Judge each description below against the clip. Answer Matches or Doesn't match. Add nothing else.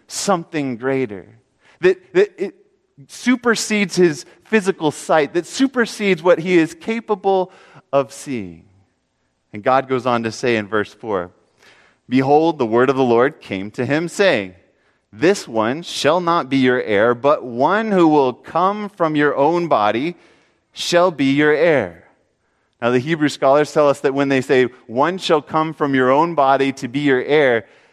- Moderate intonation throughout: Doesn't match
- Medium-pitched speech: Matches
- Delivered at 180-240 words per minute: Doesn't match